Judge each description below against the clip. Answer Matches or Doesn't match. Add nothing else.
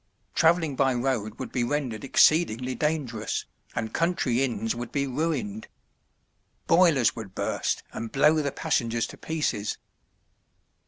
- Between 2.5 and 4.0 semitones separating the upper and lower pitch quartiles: Doesn't match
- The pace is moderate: Doesn't match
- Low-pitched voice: Matches